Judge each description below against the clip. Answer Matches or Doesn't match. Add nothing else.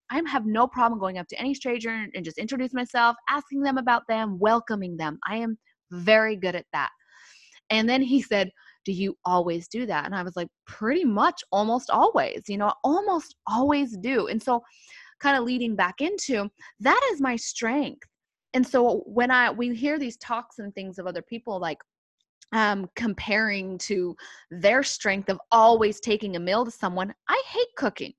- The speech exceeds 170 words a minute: Matches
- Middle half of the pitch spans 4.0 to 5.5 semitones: Matches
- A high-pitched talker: Matches